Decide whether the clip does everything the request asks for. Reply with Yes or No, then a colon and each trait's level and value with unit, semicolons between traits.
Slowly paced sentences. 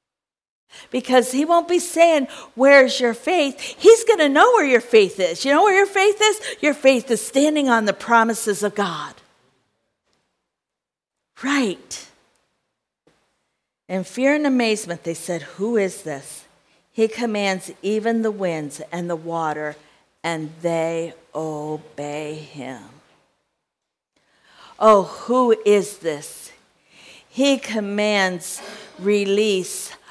Yes: slow, 120 wpm